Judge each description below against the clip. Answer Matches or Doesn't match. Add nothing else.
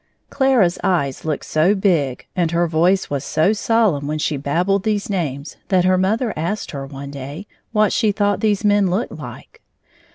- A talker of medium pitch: Matches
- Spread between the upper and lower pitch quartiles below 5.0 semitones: Doesn't match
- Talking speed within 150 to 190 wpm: Matches